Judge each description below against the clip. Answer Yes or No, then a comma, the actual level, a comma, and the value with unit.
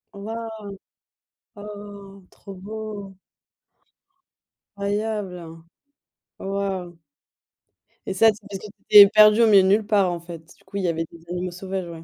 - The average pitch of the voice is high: Yes, high, 200 Hz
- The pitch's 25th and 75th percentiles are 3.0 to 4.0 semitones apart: No, narrow, 2.6 semitones